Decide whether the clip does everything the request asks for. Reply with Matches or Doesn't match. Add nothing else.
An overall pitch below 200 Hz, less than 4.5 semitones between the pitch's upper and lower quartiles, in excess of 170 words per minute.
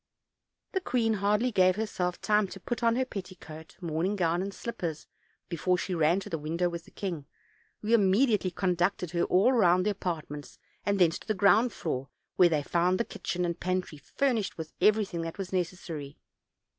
Matches